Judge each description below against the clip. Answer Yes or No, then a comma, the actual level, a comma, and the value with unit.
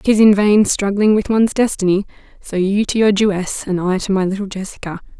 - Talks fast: No, average, 195 wpm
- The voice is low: No, high, 200 Hz